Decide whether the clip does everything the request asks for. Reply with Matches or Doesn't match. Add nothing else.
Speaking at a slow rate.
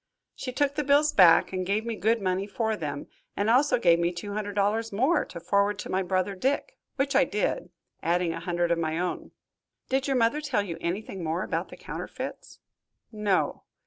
Doesn't match